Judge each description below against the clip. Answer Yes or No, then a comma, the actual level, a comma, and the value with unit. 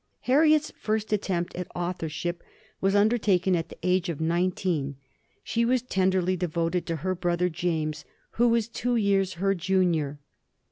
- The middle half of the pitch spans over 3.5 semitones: No, average, 3.1 semitones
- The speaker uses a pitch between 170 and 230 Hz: Yes, medium, 185 Hz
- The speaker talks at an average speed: Yes, average, 145 wpm